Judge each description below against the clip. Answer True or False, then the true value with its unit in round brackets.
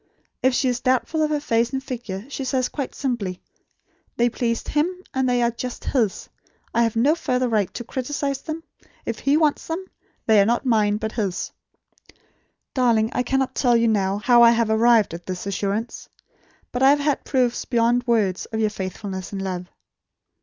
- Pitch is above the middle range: True (240 Hz)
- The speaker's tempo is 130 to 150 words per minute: False (190 wpm)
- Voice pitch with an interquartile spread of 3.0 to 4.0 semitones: True (3.4 semitones)